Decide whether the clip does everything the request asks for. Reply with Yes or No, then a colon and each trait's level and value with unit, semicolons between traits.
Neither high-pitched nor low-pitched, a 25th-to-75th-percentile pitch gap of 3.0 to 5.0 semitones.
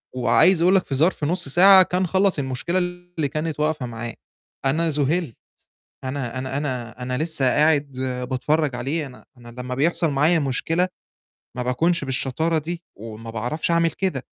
Yes: medium, 150 Hz; average, 4.7 semitones